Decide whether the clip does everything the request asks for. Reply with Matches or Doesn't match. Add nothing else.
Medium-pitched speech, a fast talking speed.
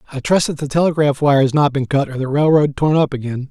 Matches